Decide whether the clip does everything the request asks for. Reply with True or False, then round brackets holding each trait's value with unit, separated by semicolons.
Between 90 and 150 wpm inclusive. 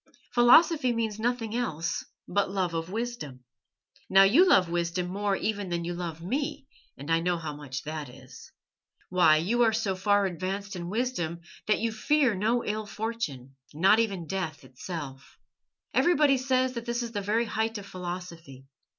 False (170 wpm)